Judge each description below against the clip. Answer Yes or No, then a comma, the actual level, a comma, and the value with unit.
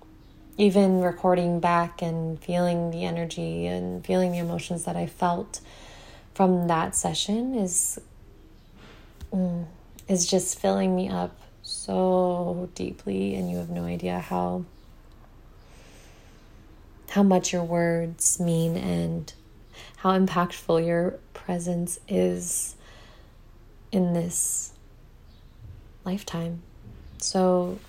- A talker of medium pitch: Yes, medium, 170 Hz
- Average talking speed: No, slow, 100 wpm